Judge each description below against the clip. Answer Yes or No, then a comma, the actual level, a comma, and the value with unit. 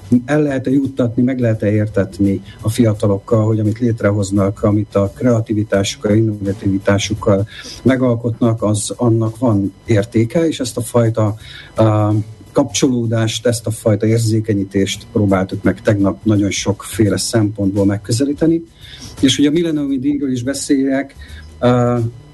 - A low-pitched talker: Yes, low, 110 Hz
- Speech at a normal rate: Yes, average, 120 wpm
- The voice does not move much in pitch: No, average, 3.3 semitones